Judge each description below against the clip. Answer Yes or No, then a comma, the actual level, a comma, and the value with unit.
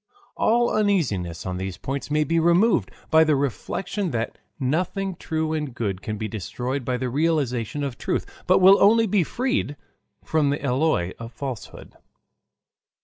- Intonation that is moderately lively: No, wide, 6.4 semitones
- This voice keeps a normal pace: Yes, average, 155 wpm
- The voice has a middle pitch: Yes, medium, 145 Hz